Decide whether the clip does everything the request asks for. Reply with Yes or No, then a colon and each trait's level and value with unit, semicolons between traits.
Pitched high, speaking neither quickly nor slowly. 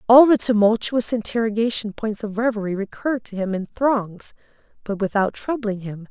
Yes: high, 220 Hz; average, 155 wpm